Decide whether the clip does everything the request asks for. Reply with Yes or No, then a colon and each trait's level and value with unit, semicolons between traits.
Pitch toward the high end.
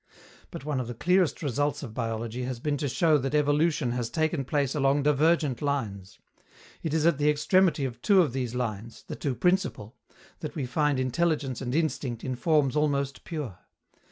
No: medium, 140 Hz